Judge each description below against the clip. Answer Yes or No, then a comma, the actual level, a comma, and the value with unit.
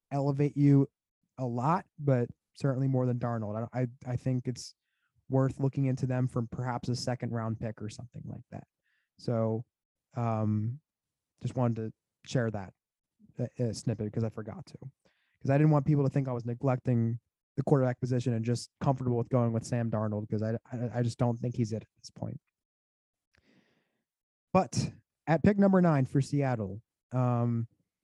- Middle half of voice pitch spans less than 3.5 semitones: Yes, average, 2.9 semitones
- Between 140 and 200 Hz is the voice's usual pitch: No, low, 125 Hz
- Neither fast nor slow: Yes, average, 175 wpm